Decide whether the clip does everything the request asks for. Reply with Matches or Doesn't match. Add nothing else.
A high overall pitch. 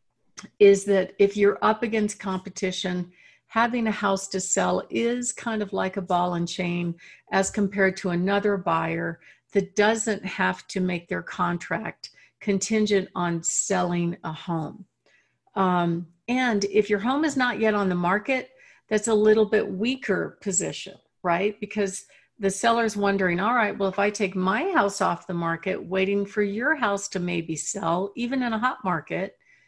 Matches